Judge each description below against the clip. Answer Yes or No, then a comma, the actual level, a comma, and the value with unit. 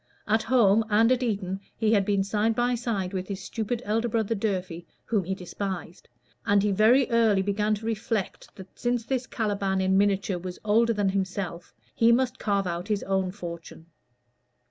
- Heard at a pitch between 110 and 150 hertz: No, high, 205 Hz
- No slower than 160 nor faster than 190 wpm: Yes, average, 180 wpm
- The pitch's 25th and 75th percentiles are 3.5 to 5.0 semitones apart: No, average, 3.0 semitones